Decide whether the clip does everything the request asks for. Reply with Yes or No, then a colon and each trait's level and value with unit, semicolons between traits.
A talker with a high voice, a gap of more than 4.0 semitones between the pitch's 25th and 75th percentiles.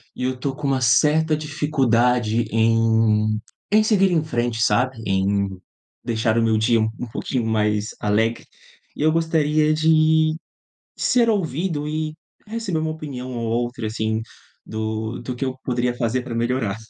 No: low, 125 Hz; wide, 5.5 semitones